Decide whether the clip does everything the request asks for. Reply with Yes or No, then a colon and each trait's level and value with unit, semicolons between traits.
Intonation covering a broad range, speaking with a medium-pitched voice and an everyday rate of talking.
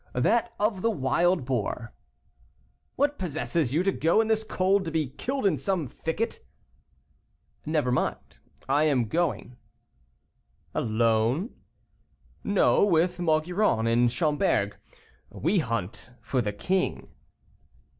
No: wide, 7.4 semitones; medium, 160 Hz; slow, 115 wpm